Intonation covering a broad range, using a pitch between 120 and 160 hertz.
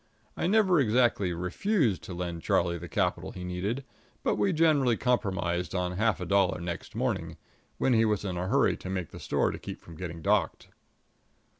No: wide, 5.8 semitones; very low, 95 Hz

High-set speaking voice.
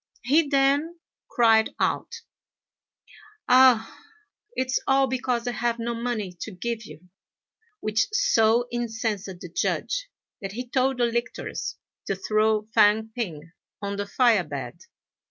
Yes: high, 230 Hz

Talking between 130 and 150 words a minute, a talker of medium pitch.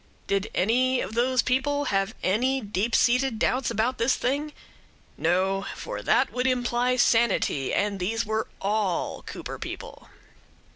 No: average, 140 wpm; high, 230 Hz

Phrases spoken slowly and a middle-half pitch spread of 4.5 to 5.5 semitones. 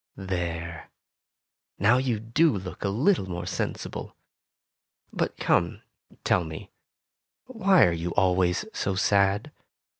Yes: slow, 115 wpm; average, 5.1 semitones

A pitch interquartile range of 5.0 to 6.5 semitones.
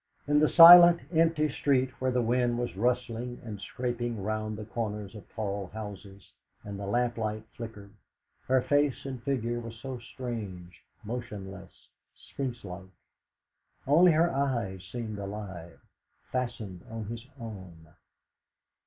No: average, 3.9 semitones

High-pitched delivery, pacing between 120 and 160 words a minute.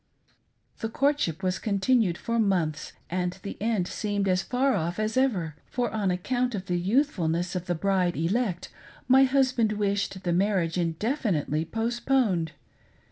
Yes: high, 200 Hz; average, 150 wpm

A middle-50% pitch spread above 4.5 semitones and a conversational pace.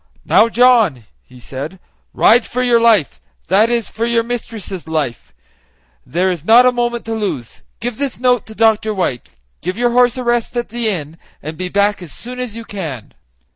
Yes: average, 5.0 semitones; average, 190 wpm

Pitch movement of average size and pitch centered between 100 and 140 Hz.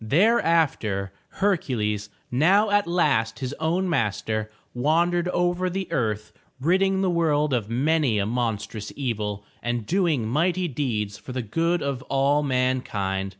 No: wide, 7.8 semitones; low, 135 Hz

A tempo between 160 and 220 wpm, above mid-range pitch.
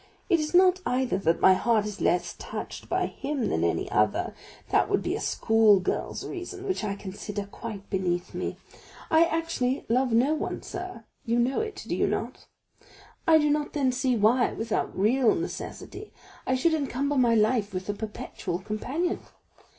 Yes: average, 175 wpm; high, 245 Hz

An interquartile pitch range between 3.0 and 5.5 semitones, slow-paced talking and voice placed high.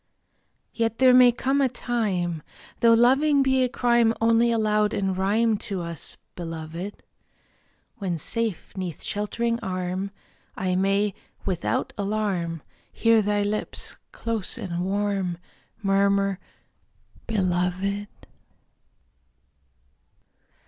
Yes: average, 3.7 semitones; slow, 100 wpm; high, 205 Hz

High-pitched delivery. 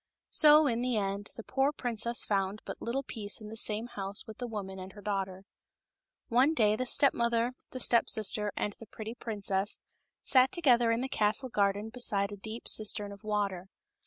Yes: high, 220 Hz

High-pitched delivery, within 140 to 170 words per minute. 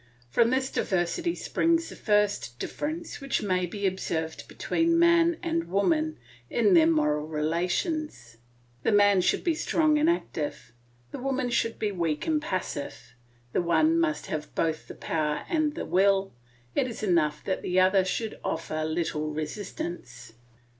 Yes: high, 200 Hz; average, 155 wpm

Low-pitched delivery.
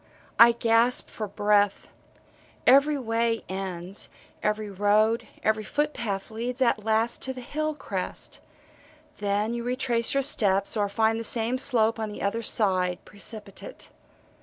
No: high, 225 Hz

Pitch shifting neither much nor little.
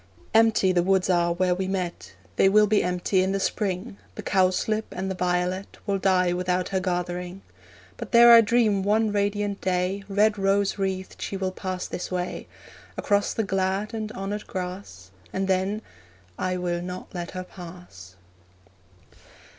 No: narrow, 1.9 semitones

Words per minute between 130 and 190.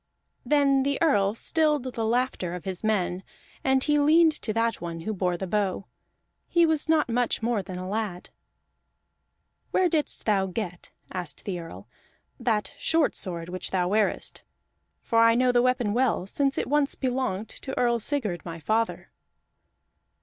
Yes: average, 165 wpm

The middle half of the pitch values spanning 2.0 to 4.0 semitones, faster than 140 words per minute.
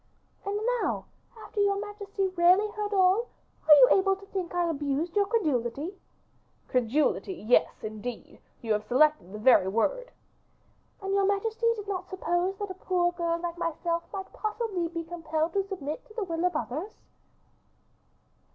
No: average, 4.6 semitones; average, 160 wpm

